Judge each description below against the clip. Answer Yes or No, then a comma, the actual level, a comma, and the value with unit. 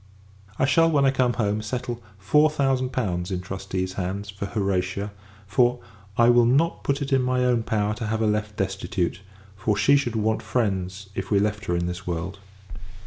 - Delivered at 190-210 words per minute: Yes, average, 195 wpm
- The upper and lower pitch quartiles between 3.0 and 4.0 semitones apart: No, average, 4.6 semitones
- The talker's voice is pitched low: Yes, low, 105 Hz